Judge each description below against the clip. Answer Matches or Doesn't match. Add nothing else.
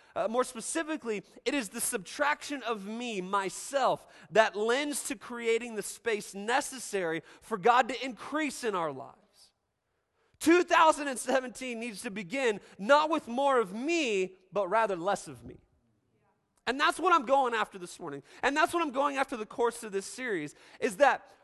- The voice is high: Matches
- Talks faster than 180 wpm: Doesn't match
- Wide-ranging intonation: Doesn't match